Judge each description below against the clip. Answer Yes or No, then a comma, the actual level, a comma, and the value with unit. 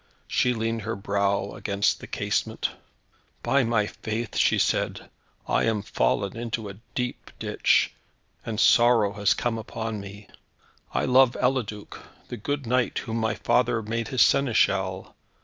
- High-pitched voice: No, low, 115 Hz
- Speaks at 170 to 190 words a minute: No, average, 145 wpm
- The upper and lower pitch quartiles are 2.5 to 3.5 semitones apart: Yes, average, 2.9 semitones